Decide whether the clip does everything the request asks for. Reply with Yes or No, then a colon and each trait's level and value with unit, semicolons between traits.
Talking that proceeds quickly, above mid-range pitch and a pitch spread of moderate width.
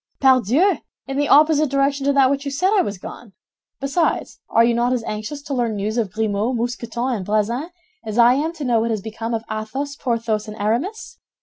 Yes: fast, 210 wpm; high, 240 Hz; average, 4.2 semitones